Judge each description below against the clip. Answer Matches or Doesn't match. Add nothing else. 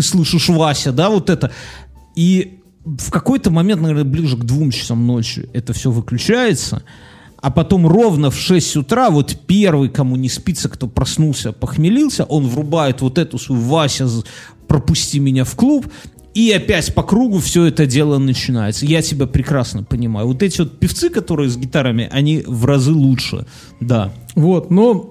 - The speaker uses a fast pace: Matches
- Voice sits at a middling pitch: Matches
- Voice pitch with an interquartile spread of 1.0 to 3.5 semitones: Doesn't match